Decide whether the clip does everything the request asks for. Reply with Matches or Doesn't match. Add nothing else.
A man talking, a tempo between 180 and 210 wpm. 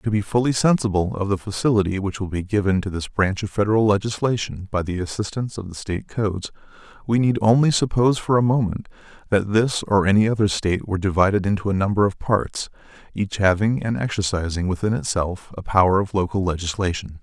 Matches